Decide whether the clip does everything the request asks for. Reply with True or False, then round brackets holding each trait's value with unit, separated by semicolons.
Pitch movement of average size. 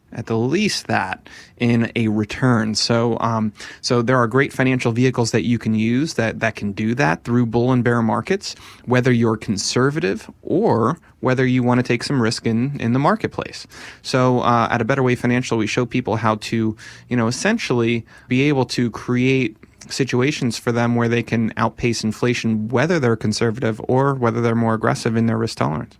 False (1.8 semitones)